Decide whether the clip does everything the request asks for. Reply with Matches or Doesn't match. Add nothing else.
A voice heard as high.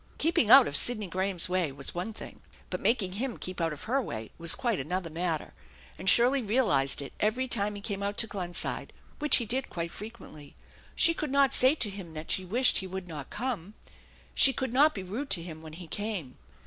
Matches